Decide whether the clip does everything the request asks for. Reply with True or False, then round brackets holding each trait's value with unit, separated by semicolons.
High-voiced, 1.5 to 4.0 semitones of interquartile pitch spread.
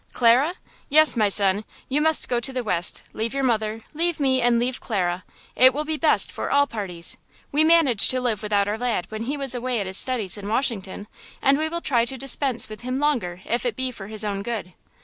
False (240 Hz; 4.6 semitones)